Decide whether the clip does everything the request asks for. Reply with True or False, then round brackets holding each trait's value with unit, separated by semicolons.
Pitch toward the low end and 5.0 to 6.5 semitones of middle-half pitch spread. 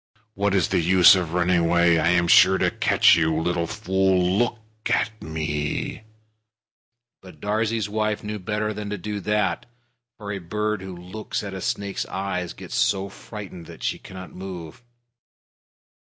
False (95 Hz; 3.3 semitones)